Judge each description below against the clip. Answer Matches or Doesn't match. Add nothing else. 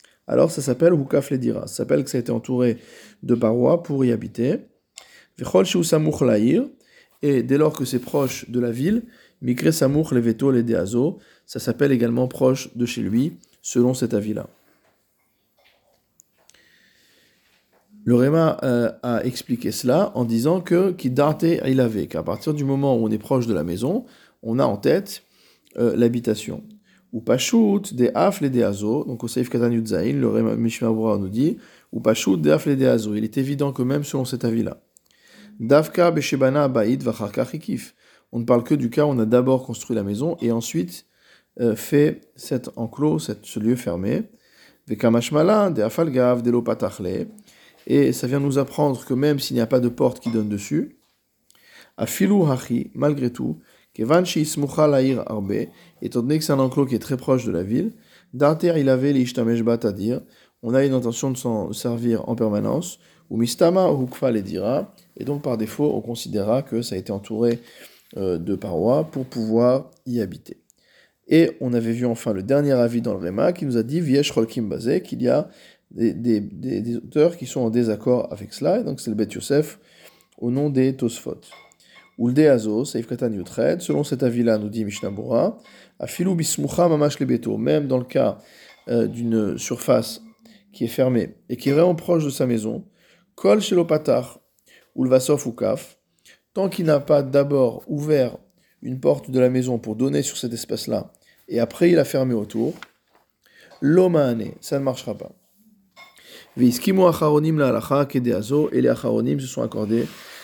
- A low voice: Matches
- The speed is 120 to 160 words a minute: Doesn't match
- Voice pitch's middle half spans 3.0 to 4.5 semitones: Matches